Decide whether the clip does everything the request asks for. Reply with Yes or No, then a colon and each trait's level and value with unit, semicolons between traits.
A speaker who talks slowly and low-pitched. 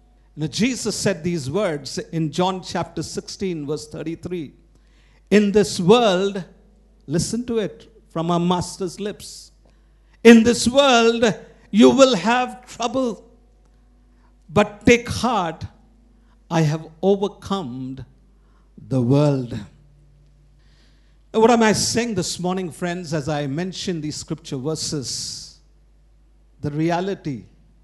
No: slow, 110 wpm; medium, 180 Hz